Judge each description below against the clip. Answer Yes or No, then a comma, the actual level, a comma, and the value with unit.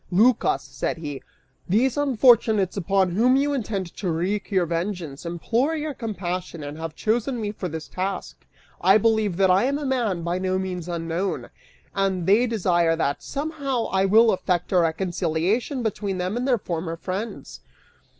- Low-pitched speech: No, high, 195 Hz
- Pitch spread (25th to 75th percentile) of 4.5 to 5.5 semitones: Yes, average, 4.9 semitones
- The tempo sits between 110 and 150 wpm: No, average, 165 wpm